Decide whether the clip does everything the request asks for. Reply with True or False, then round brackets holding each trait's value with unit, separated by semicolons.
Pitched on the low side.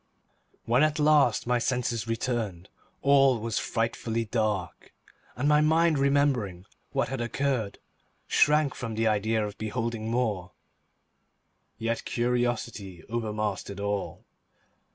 True (115 Hz)